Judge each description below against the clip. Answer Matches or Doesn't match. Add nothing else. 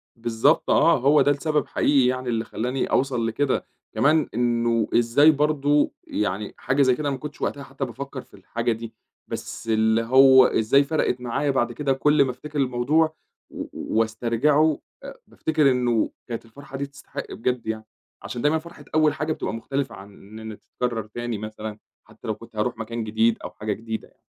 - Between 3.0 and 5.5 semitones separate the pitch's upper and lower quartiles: Matches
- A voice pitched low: Matches